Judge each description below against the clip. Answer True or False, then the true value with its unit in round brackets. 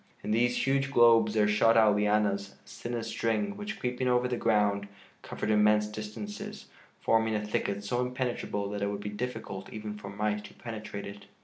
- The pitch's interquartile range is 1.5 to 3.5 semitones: True (2.8 semitones)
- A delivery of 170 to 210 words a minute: True (190 wpm)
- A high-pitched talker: False (110 Hz)